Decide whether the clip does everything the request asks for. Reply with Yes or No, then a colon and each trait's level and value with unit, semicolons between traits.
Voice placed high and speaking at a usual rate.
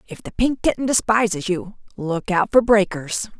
Yes: high, 195 Hz; average, 175 wpm